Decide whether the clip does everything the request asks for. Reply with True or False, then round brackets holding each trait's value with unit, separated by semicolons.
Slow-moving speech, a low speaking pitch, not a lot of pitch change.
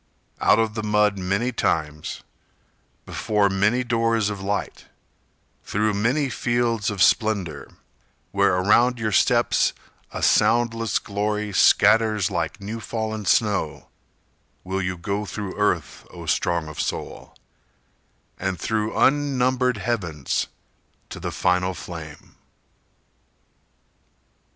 False (110 wpm; 105 Hz; 3.5 semitones)